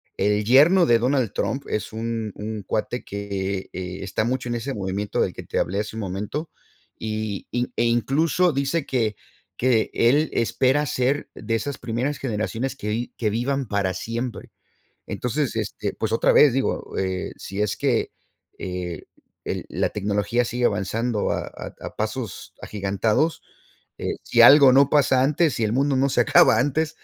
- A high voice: No, low, 115 Hz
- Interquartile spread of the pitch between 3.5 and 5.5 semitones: Yes, average, 4.4 semitones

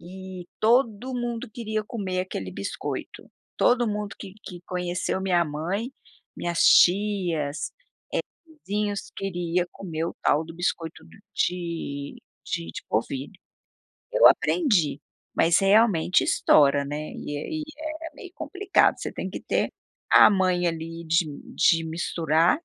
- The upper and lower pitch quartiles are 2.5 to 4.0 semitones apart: No, average, 4.4 semitones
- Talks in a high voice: No, medium, 180 Hz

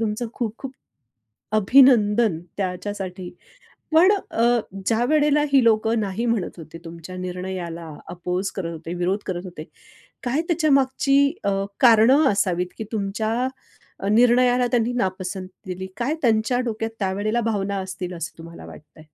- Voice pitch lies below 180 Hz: No, high, 215 Hz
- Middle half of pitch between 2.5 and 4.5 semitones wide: No, average, 5.0 semitones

